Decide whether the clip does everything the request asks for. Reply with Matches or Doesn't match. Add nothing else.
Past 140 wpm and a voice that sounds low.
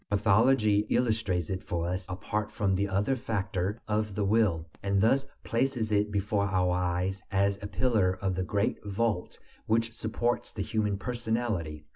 Matches